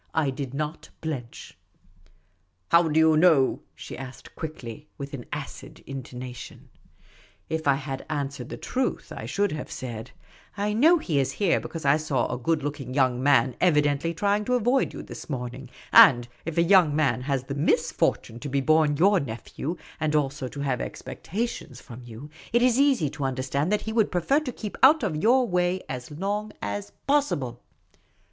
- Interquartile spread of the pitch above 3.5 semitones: Yes, wide, 5.4 semitones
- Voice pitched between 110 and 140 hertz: No, medium, 150 Hz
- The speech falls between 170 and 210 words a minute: Yes, average, 185 wpm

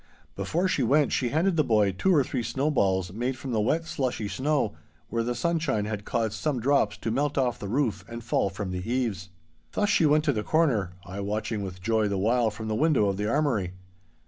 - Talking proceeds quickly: Yes, fast, 220 wpm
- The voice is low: Yes, low, 115 Hz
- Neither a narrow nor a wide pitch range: No, wide, 5.7 semitones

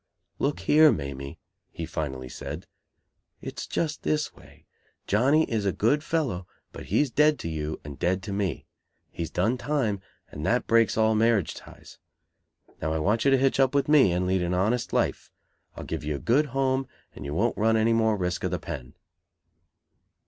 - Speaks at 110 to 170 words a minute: No, average, 185 wpm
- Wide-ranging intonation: Yes, wide, 7.9 semitones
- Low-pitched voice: Yes, low, 110 Hz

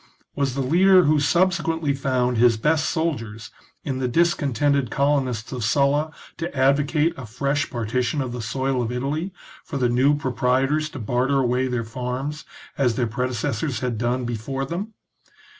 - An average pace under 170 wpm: Yes, average, 160 wpm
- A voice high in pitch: No, low, 135 Hz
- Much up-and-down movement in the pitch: No, average, 3.2 semitones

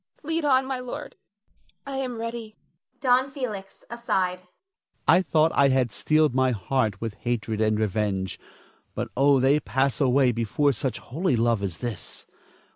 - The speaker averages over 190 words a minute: No, average, 150 wpm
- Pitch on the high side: No, medium, 140 Hz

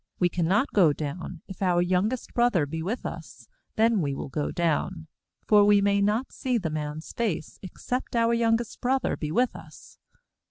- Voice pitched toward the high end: Yes, high, 195 Hz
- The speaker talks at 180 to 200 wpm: Yes, average, 190 wpm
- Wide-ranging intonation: Yes, wide, 6.0 semitones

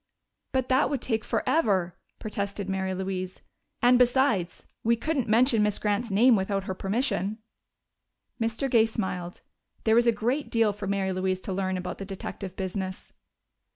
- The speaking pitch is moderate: No, high, 205 Hz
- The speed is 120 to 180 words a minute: Yes, average, 155 wpm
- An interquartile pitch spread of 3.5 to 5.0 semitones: Yes, average, 3.8 semitones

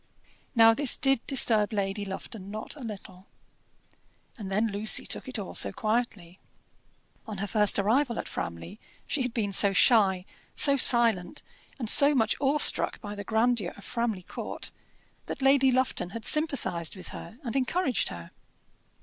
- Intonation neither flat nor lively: Yes, average, 4.4 semitones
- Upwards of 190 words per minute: No, average, 160 wpm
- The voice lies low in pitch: No, high, 220 Hz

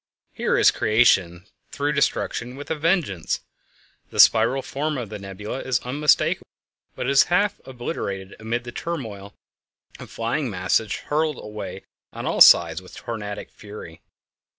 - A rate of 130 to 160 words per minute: Yes, average, 150 wpm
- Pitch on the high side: No, low, 120 Hz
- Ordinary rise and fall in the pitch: No, wide, 5.8 semitones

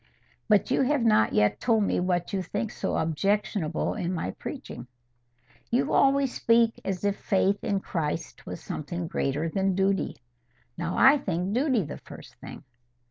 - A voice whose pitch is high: Yes, high, 195 Hz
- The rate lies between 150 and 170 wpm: Yes, average, 160 wpm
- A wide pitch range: No, average, 5.0 semitones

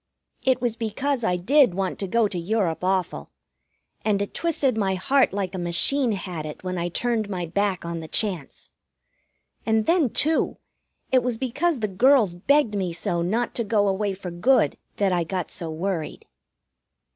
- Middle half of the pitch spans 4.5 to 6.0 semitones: Yes, average, 5.2 semitones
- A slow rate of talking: No, average, 180 wpm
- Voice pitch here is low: No, high, 200 Hz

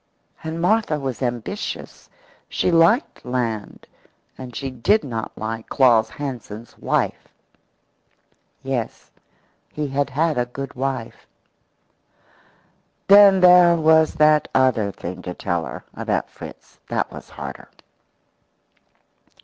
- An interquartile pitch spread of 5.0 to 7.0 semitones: Yes, wide, 5.4 semitones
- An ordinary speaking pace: No, slow, 110 wpm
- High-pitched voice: No, low, 135 Hz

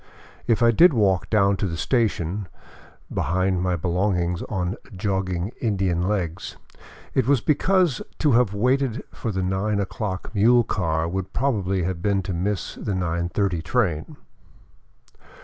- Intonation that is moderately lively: Yes, average, 3.8 semitones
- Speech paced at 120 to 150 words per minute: Yes, average, 145 wpm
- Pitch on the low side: Yes, very low, 95 Hz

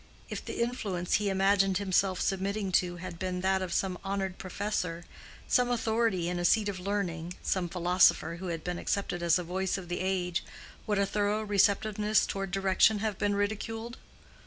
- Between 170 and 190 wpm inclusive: Yes, average, 180 wpm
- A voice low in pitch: No, high, 190 Hz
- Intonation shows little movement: Yes, narrow, 2.3 semitones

